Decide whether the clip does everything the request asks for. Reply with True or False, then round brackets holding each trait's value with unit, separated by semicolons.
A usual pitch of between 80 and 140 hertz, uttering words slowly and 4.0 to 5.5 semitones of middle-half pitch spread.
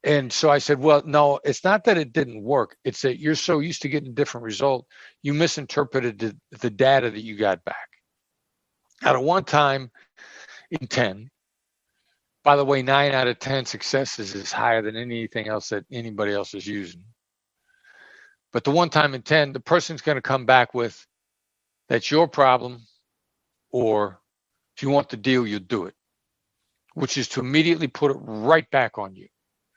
False (135 Hz; 180 wpm; 4.3 semitones)